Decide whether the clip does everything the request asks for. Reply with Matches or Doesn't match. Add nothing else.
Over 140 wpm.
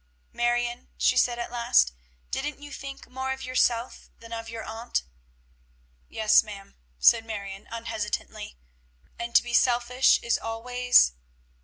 Doesn't match